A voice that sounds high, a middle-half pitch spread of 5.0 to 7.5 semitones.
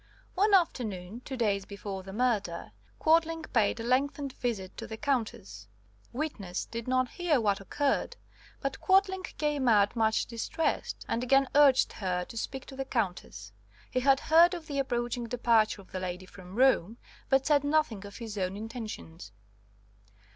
Yes: high, 240 Hz; wide, 5.6 semitones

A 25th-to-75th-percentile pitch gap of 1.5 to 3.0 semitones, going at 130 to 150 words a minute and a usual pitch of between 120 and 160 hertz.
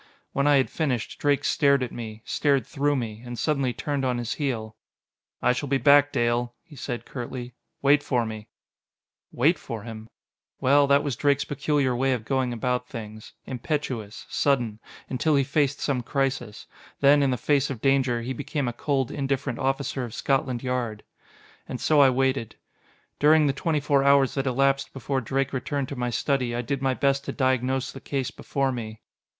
No: narrow, 2.5 semitones; average, 185 wpm; low, 135 Hz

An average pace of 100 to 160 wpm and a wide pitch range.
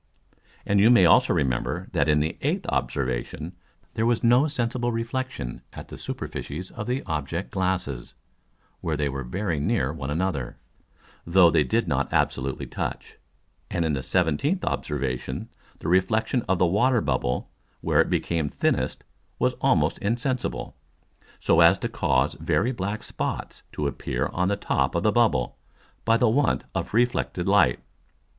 Yes: average, 155 wpm; wide, 7.8 semitones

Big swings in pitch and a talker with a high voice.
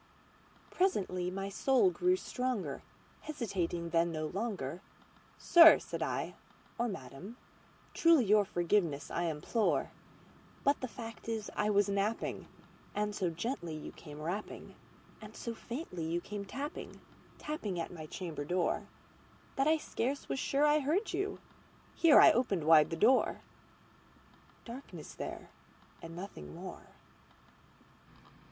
Yes: wide, 7.3 semitones; high, 205 Hz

